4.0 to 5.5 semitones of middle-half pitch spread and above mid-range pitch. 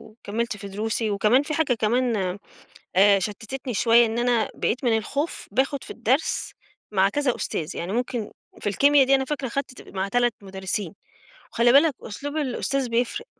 Yes: average, 4.3 semitones; high, 235 Hz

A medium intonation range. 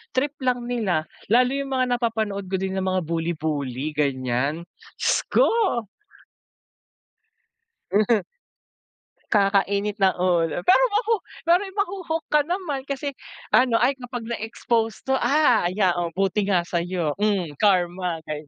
No: wide, 6.7 semitones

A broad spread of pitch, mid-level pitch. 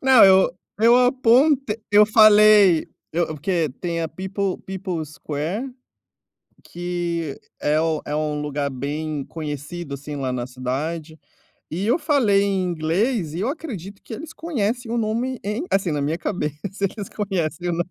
Yes: wide, 5.7 semitones; medium, 180 Hz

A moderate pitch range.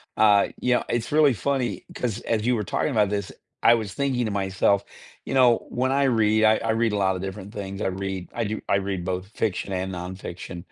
Yes: average, 3.6 semitones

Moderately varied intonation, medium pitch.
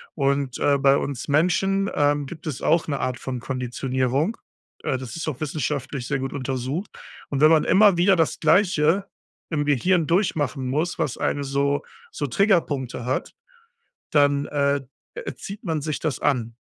Yes: average, 3.5 semitones; medium, 145 Hz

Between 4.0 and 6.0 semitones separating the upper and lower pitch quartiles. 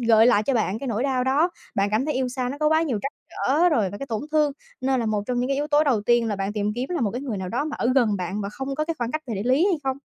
Yes: average, 4.8 semitones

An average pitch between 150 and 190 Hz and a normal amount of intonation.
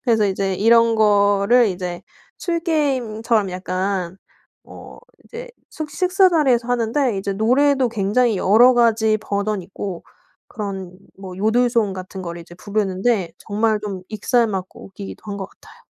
No: high, 215 Hz; average, 3.9 semitones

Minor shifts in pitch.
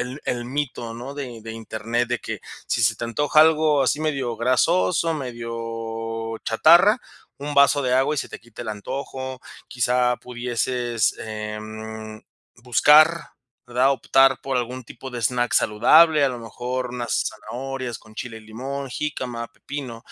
No: average, 3.2 semitones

